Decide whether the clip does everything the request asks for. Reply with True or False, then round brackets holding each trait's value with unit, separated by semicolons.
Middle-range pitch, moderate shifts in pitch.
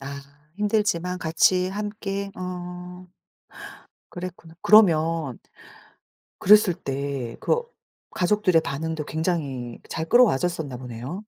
True (175 Hz; 4.8 semitones)